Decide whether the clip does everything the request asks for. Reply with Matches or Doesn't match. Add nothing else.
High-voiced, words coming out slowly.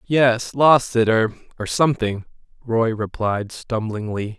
Doesn't match